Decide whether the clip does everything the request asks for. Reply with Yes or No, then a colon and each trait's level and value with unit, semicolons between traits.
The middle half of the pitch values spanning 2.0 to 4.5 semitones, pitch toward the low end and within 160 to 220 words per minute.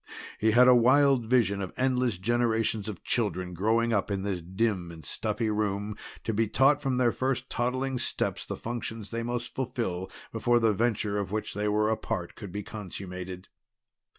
Yes: average, 3.3 semitones; low, 110 Hz; average, 180 wpm